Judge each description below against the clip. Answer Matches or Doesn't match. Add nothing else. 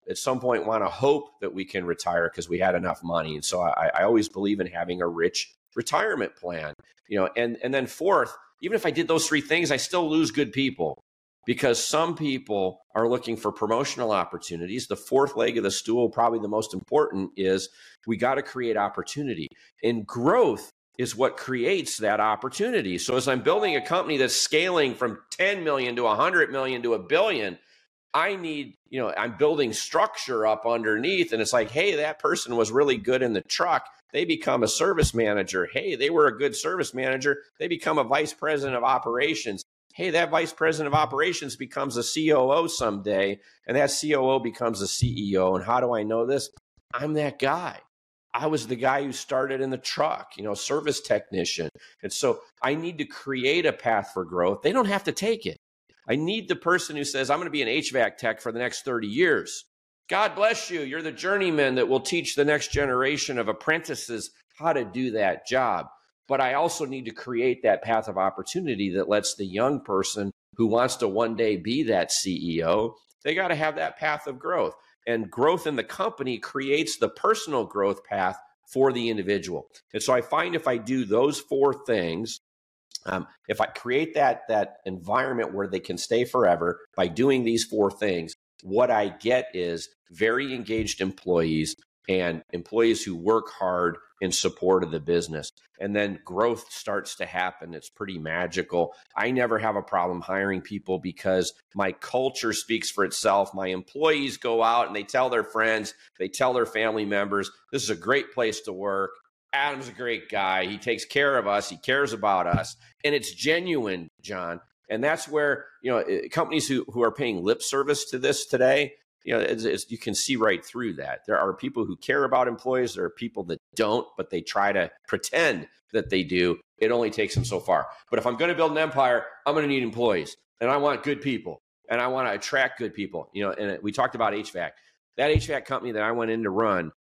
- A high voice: Doesn't match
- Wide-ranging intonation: Matches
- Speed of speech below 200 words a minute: Doesn't match